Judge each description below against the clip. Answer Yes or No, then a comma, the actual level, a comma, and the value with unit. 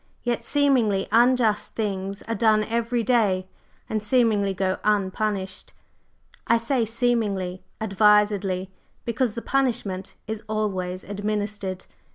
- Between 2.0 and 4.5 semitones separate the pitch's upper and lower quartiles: Yes, average, 3.1 semitones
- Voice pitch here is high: Yes, high, 210 Hz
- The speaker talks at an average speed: No, slow, 110 wpm